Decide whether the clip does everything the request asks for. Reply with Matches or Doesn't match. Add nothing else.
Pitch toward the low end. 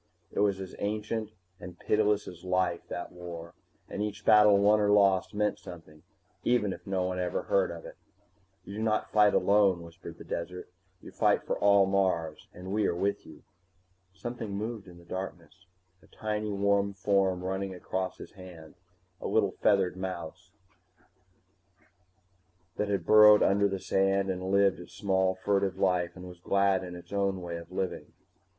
Matches